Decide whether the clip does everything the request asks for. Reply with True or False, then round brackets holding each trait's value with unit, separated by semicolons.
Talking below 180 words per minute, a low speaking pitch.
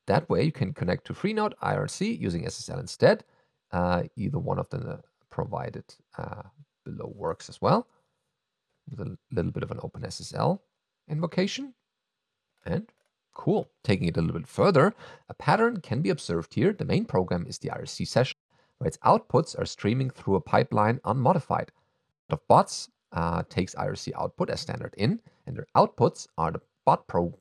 True (170 wpm; 130 Hz)